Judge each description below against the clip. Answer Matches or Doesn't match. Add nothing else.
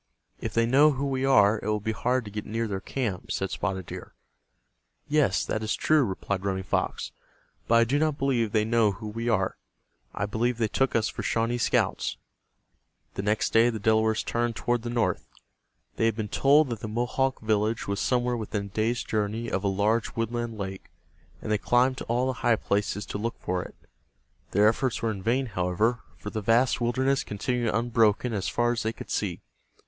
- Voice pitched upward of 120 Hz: Doesn't match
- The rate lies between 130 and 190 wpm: Doesn't match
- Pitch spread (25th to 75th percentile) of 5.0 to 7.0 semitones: Doesn't match